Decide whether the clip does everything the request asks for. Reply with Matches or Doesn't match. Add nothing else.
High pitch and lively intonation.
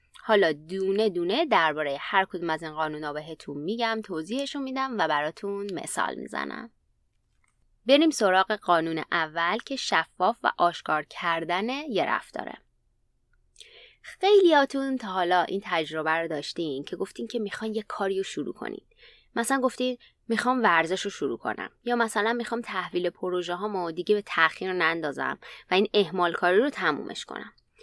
Matches